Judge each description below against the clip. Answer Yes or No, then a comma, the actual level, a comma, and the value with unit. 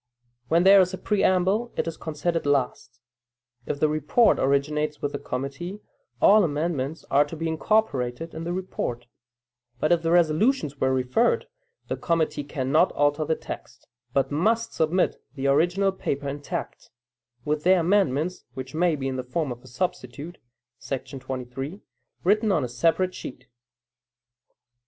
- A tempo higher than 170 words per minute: No, average, 150 wpm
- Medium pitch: Yes, medium, 155 Hz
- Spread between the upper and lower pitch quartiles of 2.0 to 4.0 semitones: No, average, 4.5 semitones